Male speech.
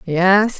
No: female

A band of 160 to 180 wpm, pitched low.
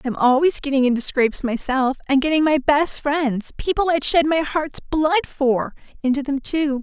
No: average, 165 wpm; very high, 280 Hz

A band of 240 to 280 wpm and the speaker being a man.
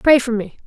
No: fast, 270 wpm; female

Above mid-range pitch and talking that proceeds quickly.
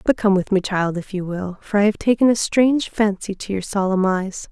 Yes: high, 200 Hz; fast, 255 wpm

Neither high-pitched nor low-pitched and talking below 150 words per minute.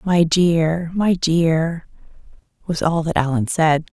Yes: medium, 165 Hz; slow, 135 wpm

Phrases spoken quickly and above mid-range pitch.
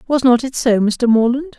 Yes: fast, 225 wpm; very high, 250 Hz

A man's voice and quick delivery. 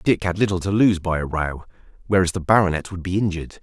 Yes: male; fast, 230 wpm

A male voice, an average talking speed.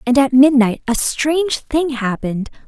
No: female; average, 155 wpm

